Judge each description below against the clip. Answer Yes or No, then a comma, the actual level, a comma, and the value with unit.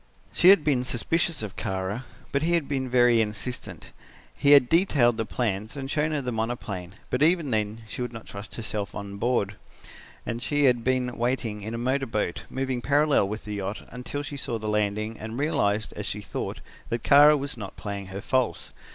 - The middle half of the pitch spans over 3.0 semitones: Yes, average, 4.7 semitones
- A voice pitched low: Yes, low, 120 Hz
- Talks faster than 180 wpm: Yes, average, 200 wpm